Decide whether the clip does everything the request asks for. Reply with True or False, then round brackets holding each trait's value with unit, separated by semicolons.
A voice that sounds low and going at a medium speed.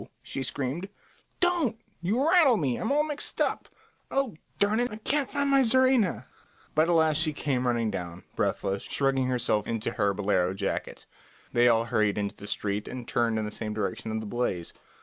True (130 Hz; 185 wpm)